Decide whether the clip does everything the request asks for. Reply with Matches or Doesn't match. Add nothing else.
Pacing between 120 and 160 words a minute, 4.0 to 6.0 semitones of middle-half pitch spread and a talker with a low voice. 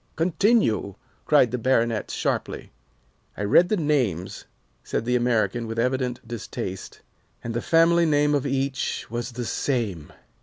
Matches